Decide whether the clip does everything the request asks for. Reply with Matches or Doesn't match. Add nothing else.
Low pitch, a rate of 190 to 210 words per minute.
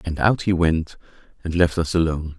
Matches